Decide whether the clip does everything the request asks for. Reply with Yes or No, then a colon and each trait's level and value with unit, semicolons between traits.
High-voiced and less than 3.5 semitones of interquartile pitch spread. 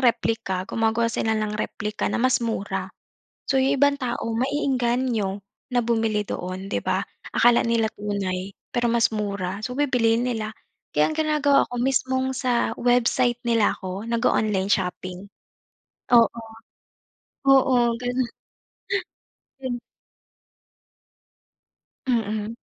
Yes: high, 235 Hz; average, 3.1 semitones